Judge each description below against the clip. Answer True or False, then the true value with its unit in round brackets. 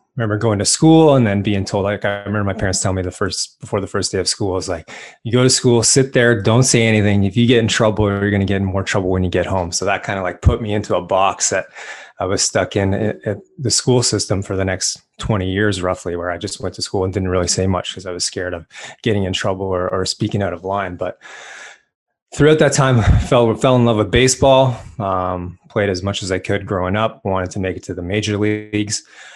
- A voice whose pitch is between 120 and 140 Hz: False (100 Hz)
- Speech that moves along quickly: True (265 wpm)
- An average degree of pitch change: True (3.3 semitones)